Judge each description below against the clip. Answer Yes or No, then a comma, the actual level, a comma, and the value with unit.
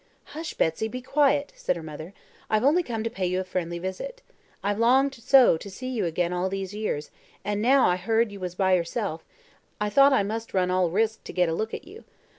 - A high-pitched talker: Yes, high, 205 Hz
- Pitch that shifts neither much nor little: No, wide, 5.7 semitones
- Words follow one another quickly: Yes, fast, 230 wpm